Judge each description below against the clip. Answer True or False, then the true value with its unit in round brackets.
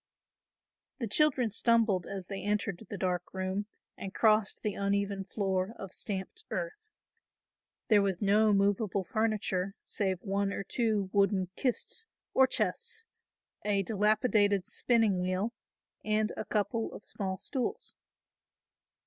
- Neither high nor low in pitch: False (205 Hz)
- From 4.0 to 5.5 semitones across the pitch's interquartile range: False (2.4 semitones)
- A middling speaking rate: False (125 wpm)